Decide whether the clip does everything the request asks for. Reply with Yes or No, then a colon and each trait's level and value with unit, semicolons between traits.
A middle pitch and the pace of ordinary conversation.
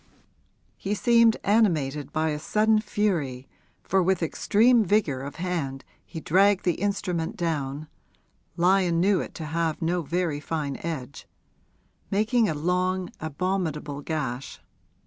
No: medium, 170 Hz; slow, 125 wpm